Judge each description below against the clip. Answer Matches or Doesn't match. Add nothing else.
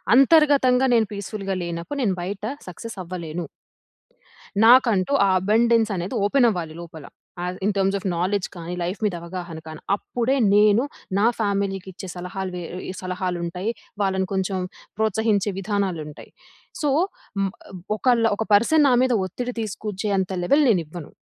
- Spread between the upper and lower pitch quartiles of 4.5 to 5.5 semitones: Doesn't match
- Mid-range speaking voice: Doesn't match